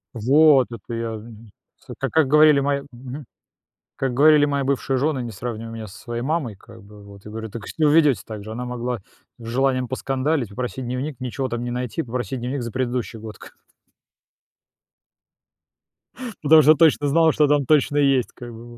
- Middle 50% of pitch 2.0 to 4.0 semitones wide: Yes, average, 3.5 semitones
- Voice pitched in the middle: No, low, 125 Hz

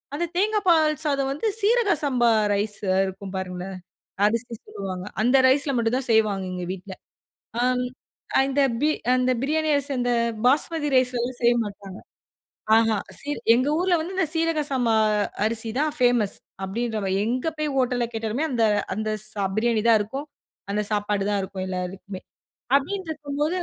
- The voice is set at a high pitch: Yes, high, 245 Hz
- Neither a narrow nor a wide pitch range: No, wide, 5.7 semitones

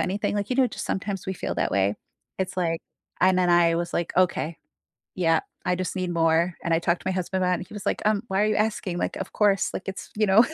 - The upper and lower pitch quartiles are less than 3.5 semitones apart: Yes, narrow, 2.5 semitones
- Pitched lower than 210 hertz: Yes, medium, 185 Hz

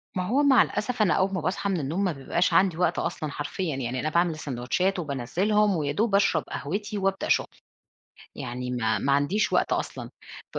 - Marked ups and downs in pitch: Yes, wide, 5.9 semitones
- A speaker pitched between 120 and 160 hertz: No, medium, 175 Hz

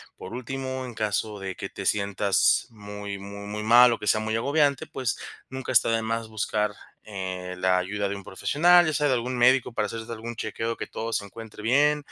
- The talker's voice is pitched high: No, low, 110 Hz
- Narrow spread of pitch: No, average, 3.6 semitones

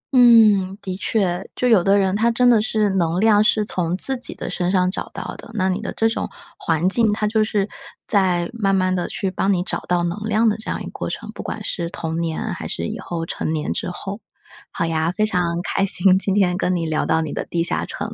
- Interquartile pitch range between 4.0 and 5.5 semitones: No, average, 3.5 semitones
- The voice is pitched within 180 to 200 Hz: Yes, high, 190 Hz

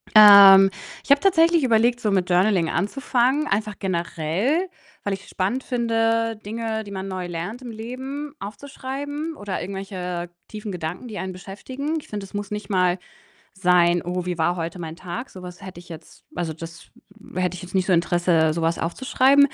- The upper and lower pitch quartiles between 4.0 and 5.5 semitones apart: Yes, average, 5.1 semitones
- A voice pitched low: No, high, 195 Hz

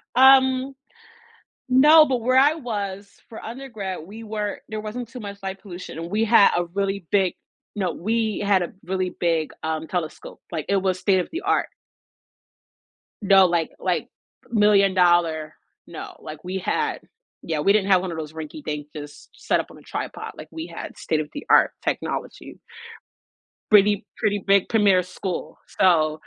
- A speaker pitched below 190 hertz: No, high, 195 Hz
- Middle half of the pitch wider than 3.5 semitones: Yes, average, 4.0 semitones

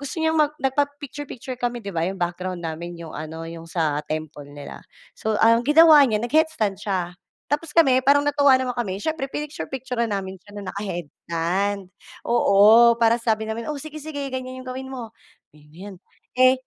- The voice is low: No, high, 230 Hz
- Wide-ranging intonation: Yes, wide, 6.9 semitones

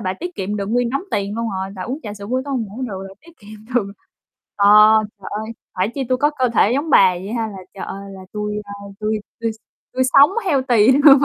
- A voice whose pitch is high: Yes, high, 220 Hz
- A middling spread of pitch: Yes, average, 4.4 semitones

